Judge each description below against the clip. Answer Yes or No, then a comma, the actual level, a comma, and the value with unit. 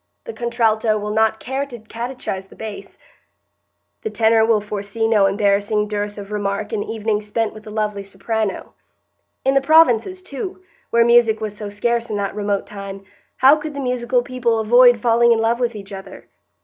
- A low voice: No, high, 220 Hz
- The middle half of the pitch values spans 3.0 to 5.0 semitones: No, narrow, 2.5 semitones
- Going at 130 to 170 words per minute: No, average, 180 wpm